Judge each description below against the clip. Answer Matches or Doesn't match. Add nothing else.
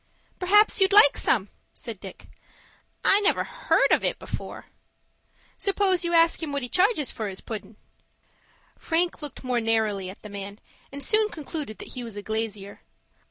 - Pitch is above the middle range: Matches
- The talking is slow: Doesn't match